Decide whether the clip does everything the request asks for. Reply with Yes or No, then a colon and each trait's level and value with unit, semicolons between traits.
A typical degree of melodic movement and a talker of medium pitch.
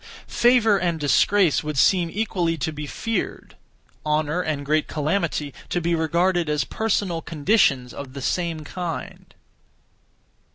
Yes: average, 3.5 semitones; medium, 165 Hz